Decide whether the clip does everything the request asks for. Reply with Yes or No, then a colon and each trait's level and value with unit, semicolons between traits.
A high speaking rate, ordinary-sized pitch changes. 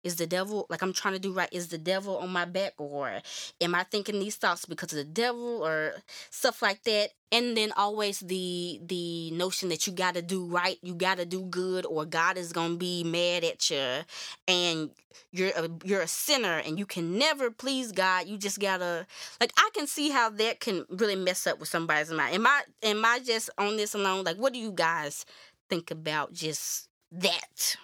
Yes: fast, 210 wpm; average, 3.5 semitones